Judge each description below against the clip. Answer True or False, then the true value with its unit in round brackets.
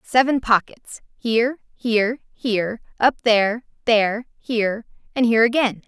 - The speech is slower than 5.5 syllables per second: True (4.9 syllables/s)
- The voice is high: True (230 Hz)